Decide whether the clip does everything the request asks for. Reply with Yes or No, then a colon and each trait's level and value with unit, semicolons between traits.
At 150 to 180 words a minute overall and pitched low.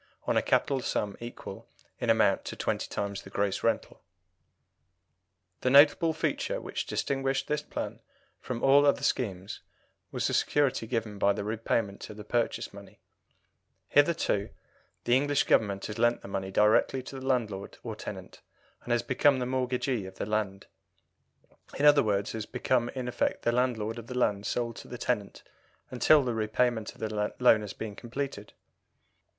Yes: average, 165 wpm; low, 120 Hz